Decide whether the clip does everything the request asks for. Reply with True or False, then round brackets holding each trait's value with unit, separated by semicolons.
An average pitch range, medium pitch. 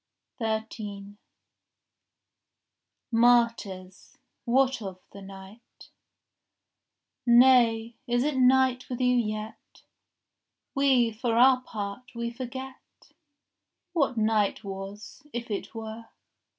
False (3.0 semitones; 230 Hz)